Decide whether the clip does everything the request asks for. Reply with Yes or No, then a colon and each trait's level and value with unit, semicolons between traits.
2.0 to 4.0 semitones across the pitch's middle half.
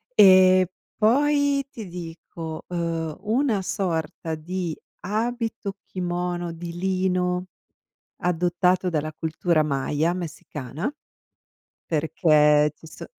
Yes: average, 2.8 semitones